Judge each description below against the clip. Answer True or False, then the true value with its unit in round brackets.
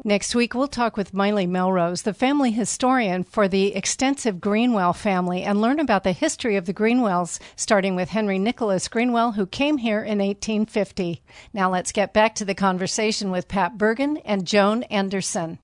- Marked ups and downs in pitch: False (3.1 semitones)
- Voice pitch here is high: True (205 Hz)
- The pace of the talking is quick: False (175 wpm)